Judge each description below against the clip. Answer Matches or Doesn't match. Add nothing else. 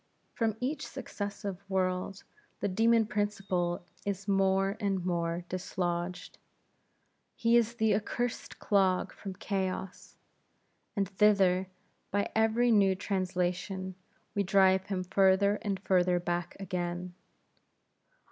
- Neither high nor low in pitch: Doesn't match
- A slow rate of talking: Matches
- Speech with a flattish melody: Matches